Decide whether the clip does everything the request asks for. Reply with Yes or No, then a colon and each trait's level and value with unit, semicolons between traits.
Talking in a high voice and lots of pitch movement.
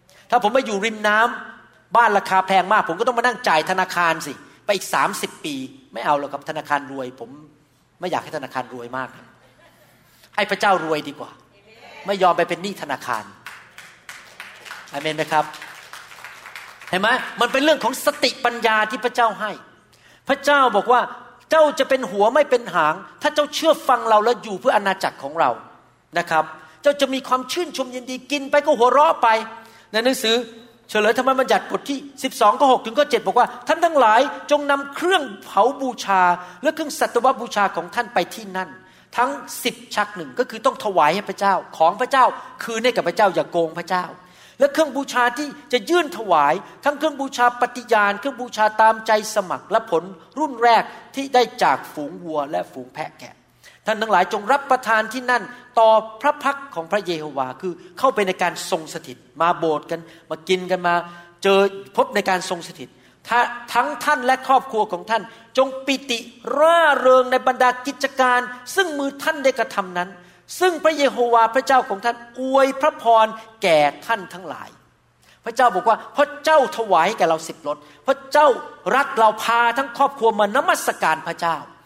Yes: high, 225 Hz; wide, 6.5 semitones